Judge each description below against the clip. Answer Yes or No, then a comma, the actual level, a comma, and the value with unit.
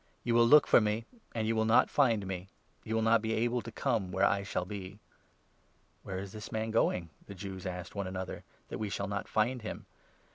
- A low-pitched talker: Yes, low, 105 Hz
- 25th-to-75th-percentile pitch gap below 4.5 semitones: Yes, average, 2.9 semitones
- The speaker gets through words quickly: Yes, fast, 245 wpm